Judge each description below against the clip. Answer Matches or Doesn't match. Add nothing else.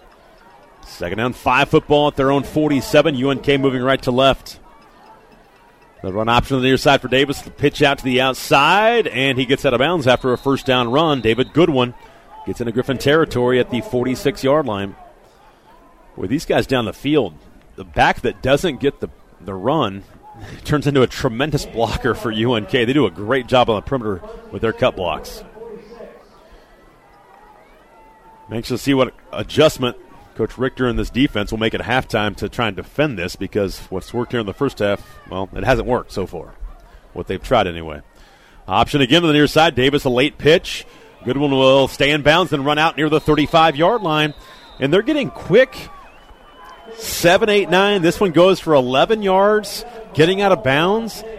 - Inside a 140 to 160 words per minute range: Doesn't match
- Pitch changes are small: Doesn't match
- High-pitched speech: Doesn't match